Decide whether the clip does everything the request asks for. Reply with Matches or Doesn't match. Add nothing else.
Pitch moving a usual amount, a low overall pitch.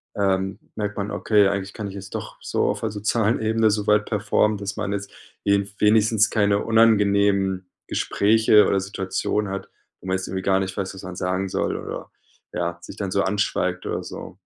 Doesn't match